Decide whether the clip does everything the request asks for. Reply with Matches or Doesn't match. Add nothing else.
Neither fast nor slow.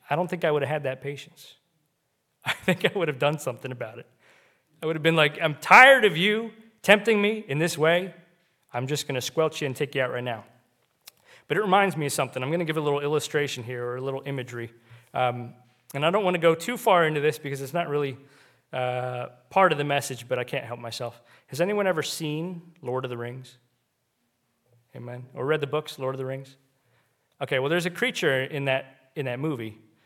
Doesn't match